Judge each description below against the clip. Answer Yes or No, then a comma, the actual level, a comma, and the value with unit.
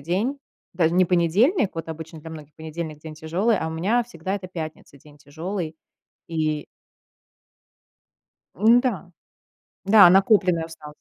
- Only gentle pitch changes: No, average, 3.7 semitones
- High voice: No, medium, 170 Hz